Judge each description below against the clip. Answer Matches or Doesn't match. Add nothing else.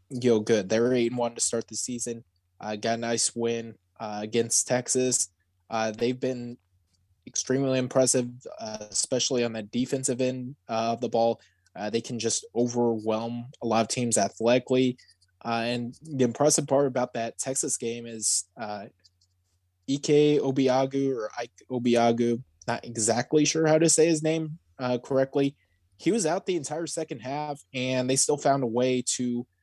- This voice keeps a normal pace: Matches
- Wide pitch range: Doesn't match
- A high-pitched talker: Doesn't match